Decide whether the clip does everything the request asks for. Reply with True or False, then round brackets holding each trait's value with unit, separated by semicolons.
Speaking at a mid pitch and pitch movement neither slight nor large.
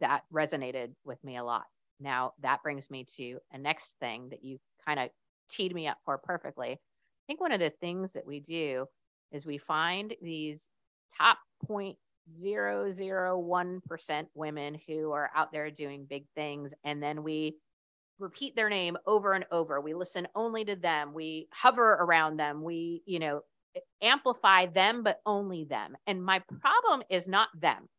True (160 Hz; 4.7 semitones)